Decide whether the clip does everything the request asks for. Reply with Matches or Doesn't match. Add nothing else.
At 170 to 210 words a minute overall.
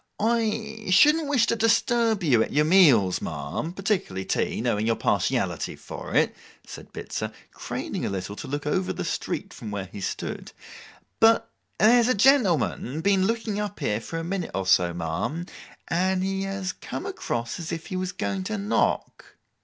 Matches